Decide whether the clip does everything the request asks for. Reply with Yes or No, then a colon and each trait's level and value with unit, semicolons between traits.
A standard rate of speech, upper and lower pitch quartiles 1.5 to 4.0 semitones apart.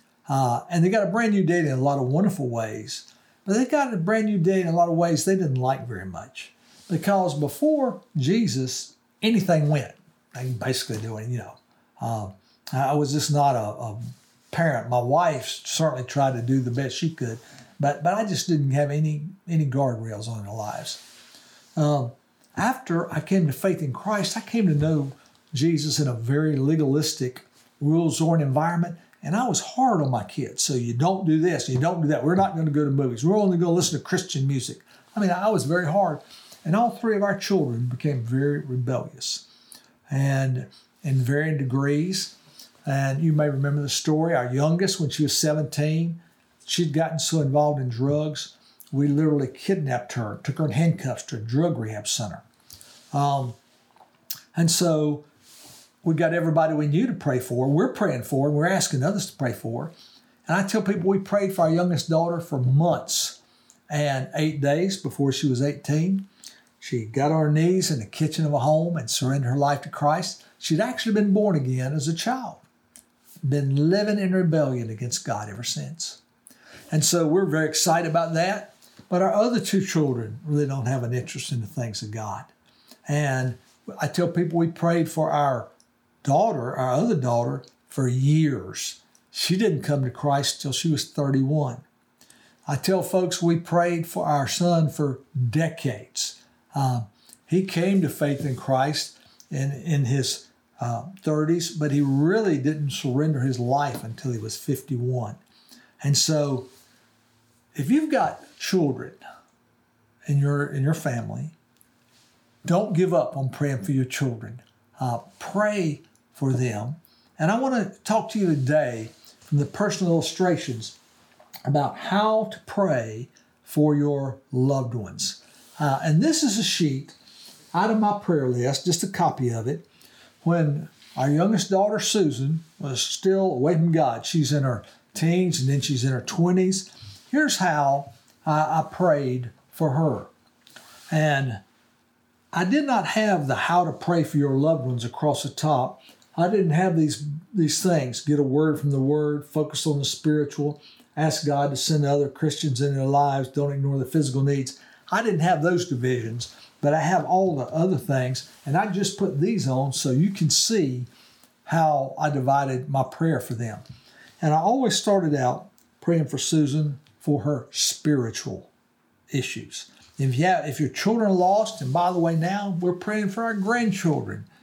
No: average, 180 wpm; average, 4.5 semitones